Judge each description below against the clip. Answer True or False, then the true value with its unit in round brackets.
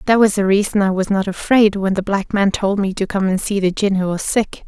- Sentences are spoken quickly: True (295 wpm)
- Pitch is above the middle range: True (200 Hz)